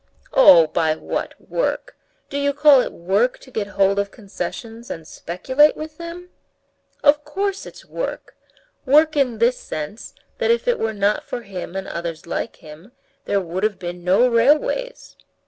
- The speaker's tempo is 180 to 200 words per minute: No, average, 165 wpm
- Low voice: No, high, 230 Hz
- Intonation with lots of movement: Yes, wide, 8.1 semitones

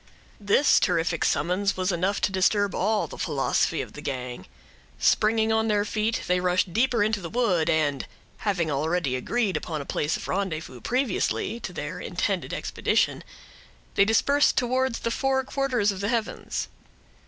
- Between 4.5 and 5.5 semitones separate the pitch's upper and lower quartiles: Yes, average, 5.2 semitones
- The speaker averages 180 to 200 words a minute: No, average, 160 wpm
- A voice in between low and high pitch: No, high, 200 Hz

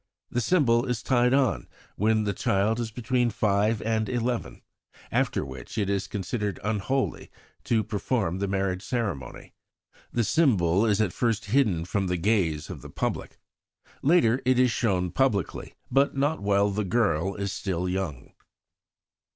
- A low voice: Yes, low, 105 Hz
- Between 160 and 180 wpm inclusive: No, average, 150 wpm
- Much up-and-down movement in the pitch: No, average, 4.0 semitones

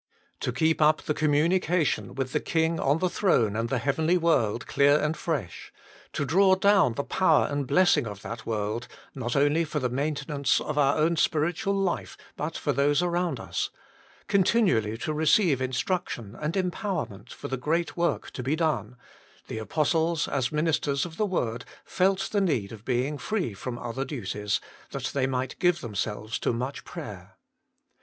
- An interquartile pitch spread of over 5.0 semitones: Yes, wide, 5.5 semitones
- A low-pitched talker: No, medium, 145 Hz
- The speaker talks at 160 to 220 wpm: Yes, average, 175 wpm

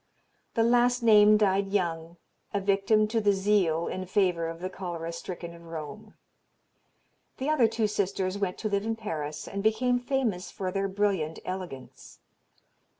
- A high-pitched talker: Yes, high, 195 Hz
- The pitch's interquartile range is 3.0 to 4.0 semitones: Yes, average, 3.7 semitones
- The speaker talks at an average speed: Yes, average, 155 wpm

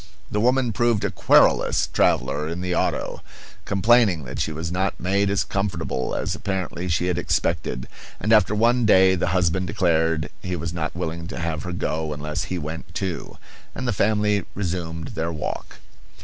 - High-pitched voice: No, very low, 90 Hz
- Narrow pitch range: No, average, 3.6 semitones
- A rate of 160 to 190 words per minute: Yes, average, 175 wpm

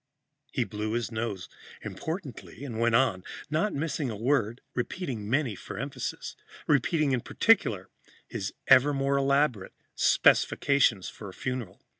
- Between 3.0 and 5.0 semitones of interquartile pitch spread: Yes, average, 4.4 semitones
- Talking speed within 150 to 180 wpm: No, average, 140 wpm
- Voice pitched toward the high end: No, low, 125 Hz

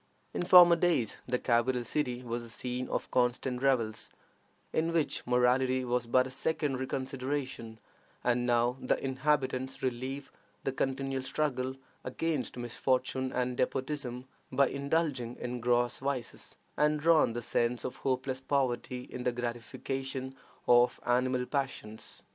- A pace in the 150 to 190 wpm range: No, slow, 135 wpm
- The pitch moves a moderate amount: No, narrow, 1.7 semitones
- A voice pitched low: Yes, low, 130 Hz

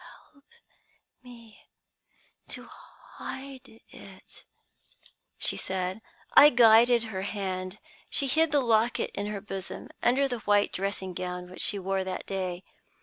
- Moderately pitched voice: No, high, 210 Hz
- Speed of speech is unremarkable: No, slow, 130 wpm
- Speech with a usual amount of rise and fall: Yes, average, 4.5 semitones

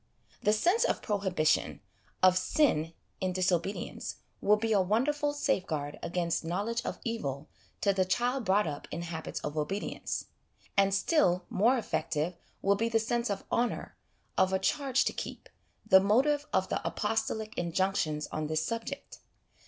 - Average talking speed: Yes, average, 155 wpm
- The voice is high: Yes, high, 195 Hz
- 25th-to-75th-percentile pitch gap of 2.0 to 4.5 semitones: No, average, 5.1 semitones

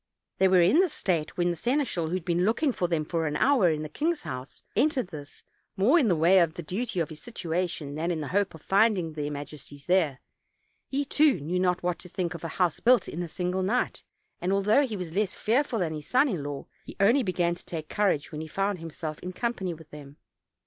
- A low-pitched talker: No, medium, 180 Hz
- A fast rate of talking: Yes, fast, 240 wpm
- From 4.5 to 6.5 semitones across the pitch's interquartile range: Yes, average, 4.8 semitones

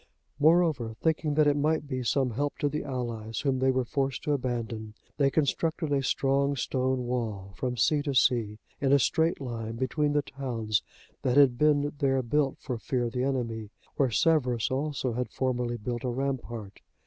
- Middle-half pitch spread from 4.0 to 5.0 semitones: No, average, 3.2 semitones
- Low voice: Yes, low, 130 Hz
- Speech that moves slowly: No, average, 185 wpm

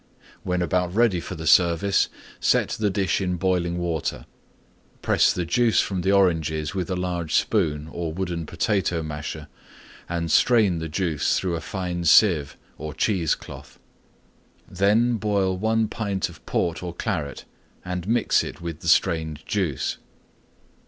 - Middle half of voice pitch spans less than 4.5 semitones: Yes, average, 3.3 semitones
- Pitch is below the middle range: Yes, very low, 90 Hz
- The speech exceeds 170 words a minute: No, average, 150 wpm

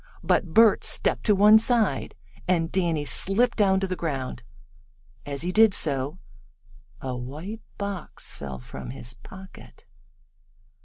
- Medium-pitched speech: Yes, medium, 180 Hz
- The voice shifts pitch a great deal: Yes, wide, 6.7 semitones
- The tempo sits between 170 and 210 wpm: No, slow, 135 wpm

